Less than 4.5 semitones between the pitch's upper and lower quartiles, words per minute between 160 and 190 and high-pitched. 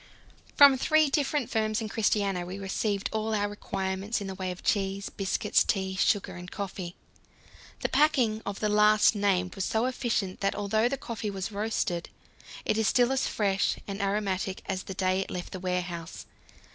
Yes: narrow, 2.6 semitones; average, 180 wpm; high, 200 Hz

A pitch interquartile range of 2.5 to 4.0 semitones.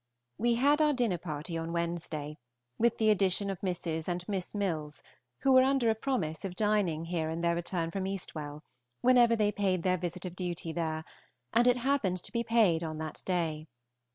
No: average, 5.2 semitones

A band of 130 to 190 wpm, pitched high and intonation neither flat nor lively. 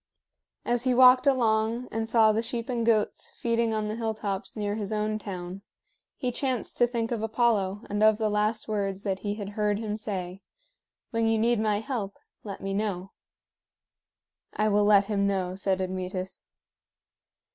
No: average, 170 wpm; high, 215 Hz; narrow, 2.3 semitones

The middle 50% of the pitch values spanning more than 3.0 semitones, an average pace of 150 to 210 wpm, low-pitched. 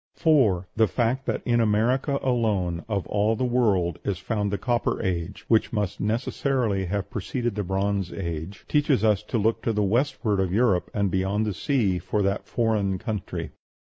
Yes: average, 3.6 semitones; average, 175 wpm; low, 105 Hz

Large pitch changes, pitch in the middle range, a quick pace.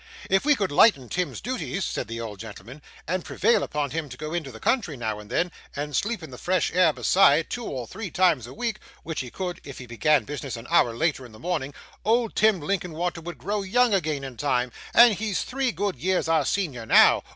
Yes: wide, 6.9 semitones; medium, 160 Hz; fast, 225 wpm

